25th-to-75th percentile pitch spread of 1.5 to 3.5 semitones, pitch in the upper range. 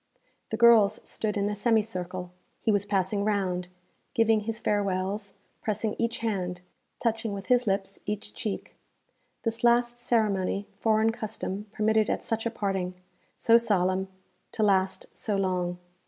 Yes: narrow, 2.6 semitones; high, 210 Hz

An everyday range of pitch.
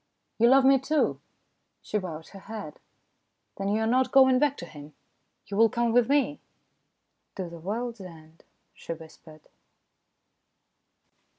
No: wide, 7.2 semitones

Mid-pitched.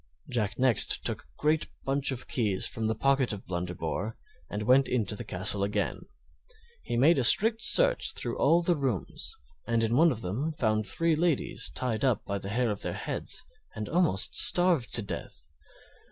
No: low, 120 Hz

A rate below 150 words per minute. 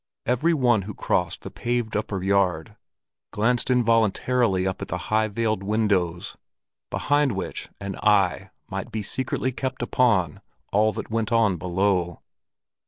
Yes: average, 140 wpm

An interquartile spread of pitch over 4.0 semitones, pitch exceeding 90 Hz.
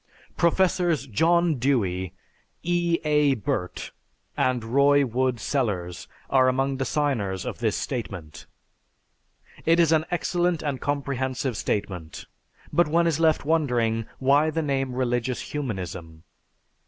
Yes: wide, 5.4 semitones; low, 135 Hz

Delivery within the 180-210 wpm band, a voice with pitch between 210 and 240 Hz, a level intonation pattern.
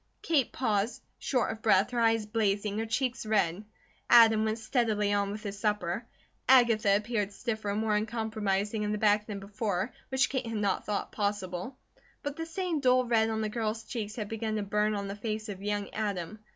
Yes: average, 195 wpm; high, 215 Hz; narrow, 1.9 semitones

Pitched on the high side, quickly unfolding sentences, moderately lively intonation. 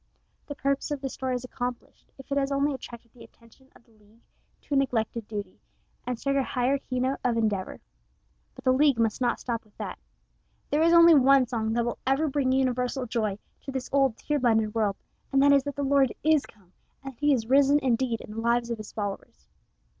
Yes: very high, 255 Hz; fast, 220 wpm; average, 3.2 semitones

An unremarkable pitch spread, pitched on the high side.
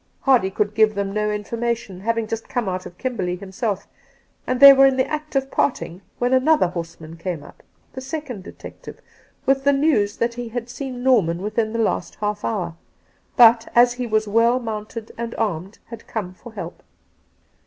Yes: average, 3.8 semitones; high, 225 Hz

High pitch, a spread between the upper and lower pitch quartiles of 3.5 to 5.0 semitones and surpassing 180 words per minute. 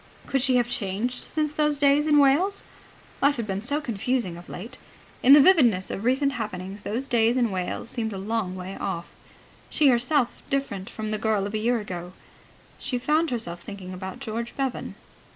No: high, 235 Hz; wide, 5.6 semitones; average, 190 wpm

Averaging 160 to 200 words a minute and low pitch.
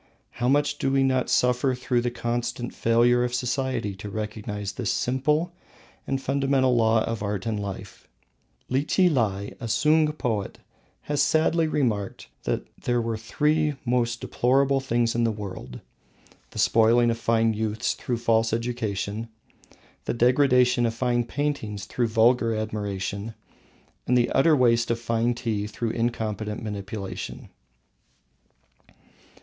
No: slow, 135 wpm; low, 120 Hz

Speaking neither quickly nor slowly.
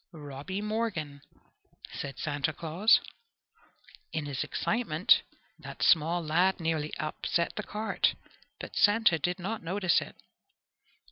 No: slow, 115 wpm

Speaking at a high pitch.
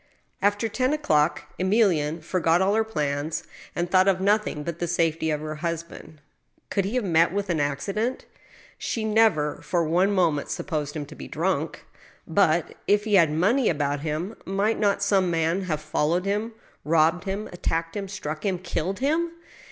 No: medium, 175 Hz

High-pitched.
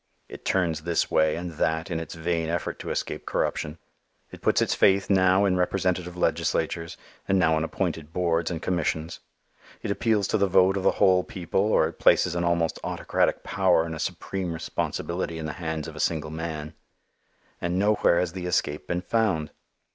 No: very low, 85 Hz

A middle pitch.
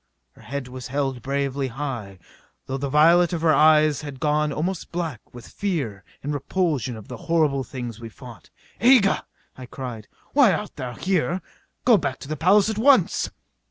Yes: medium, 145 Hz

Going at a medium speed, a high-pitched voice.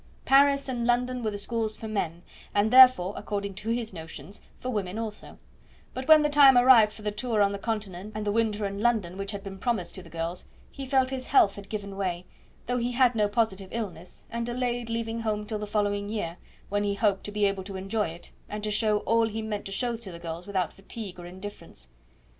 No: fast, 230 wpm; high, 210 Hz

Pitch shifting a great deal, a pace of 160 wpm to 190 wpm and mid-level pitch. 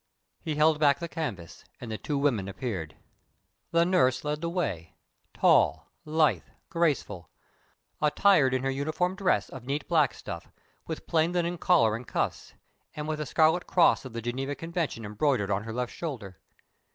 Yes: wide, 6.0 semitones; average, 165 wpm; medium, 145 Hz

